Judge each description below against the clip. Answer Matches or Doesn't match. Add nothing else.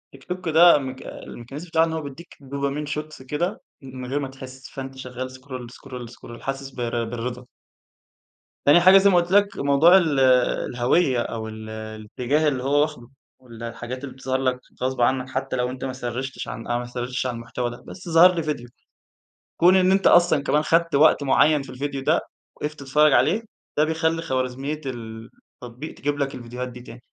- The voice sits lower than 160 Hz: Matches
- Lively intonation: Doesn't match